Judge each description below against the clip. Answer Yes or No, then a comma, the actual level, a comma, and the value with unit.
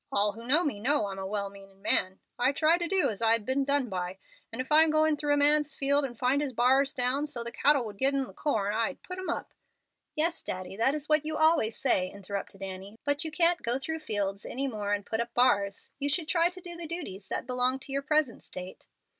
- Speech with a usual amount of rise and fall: No, wide, 6.6 semitones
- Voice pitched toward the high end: Yes, very high, 260 Hz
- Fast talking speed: Yes, fast, 250 wpm